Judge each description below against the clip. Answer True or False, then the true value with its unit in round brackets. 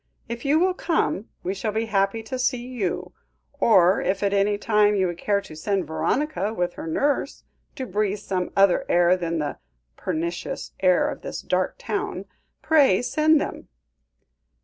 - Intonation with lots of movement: True (5.7 semitones)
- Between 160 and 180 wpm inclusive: True (170 wpm)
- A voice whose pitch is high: True (205 Hz)